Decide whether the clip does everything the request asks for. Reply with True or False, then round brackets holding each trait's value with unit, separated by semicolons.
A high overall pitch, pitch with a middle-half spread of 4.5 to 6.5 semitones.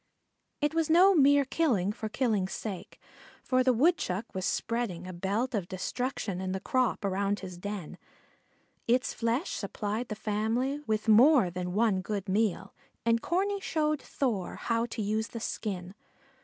True (220 Hz; 4.8 semitones)